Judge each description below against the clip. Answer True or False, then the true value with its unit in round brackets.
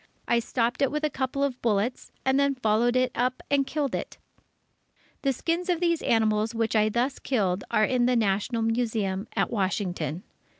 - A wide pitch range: False (3.7 semitones)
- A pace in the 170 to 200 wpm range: True (185 wpm)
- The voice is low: False (240 Hz)